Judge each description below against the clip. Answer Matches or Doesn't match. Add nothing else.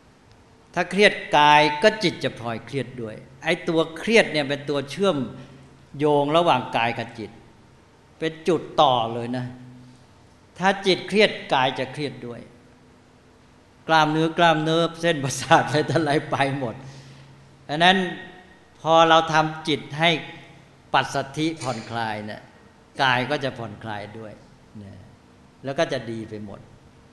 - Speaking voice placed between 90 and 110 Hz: Doesn't match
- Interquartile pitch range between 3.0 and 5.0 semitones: Doesn't match